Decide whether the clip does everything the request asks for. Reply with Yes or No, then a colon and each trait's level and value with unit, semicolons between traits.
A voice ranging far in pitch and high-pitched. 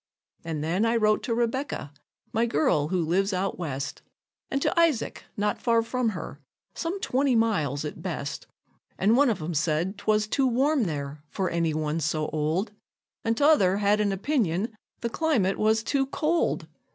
Yes: wide, 6.4 semitones; high, 205 Hz